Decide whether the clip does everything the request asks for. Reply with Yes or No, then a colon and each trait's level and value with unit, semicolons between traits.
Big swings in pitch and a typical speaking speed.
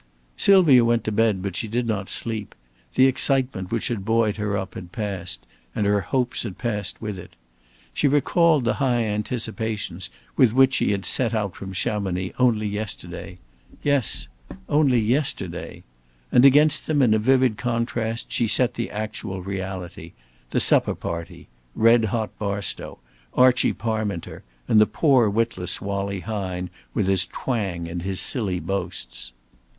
No: average, 3.9 semitones; average, 155 wpm